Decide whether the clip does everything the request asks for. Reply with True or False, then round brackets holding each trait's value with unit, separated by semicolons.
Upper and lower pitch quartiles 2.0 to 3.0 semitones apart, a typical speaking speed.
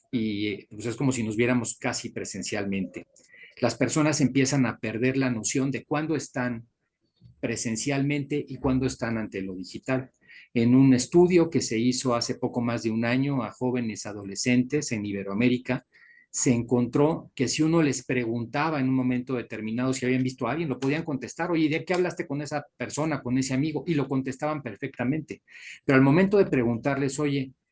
False (3.6 semitones; 180 wpm)